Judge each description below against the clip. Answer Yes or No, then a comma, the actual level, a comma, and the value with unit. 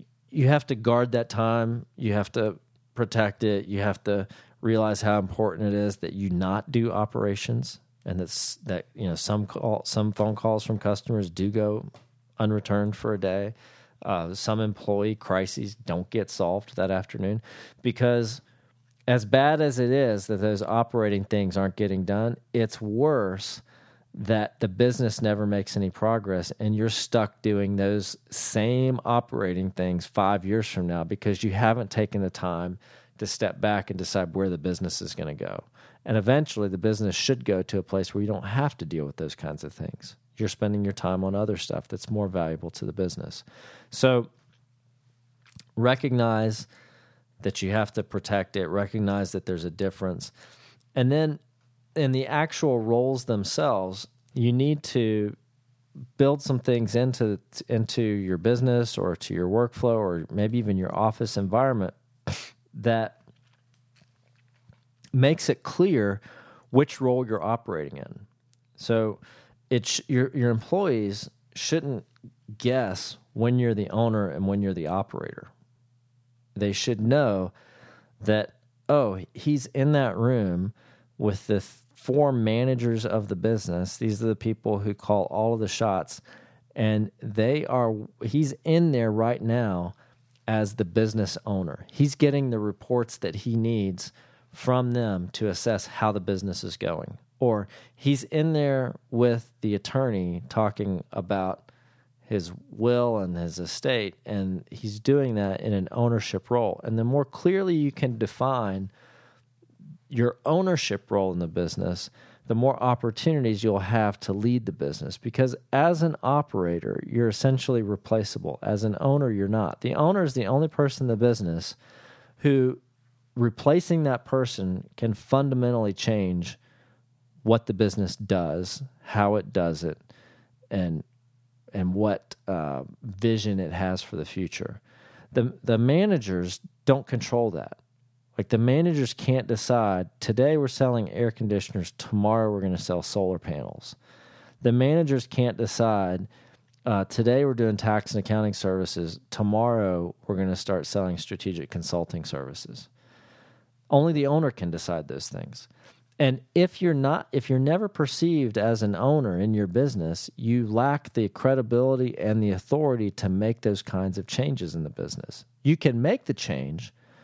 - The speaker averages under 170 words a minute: Yes, average, 155 wpm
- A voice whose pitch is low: Yes, low, 115 Hz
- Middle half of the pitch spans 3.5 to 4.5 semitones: Yes, average, 3.8 semitones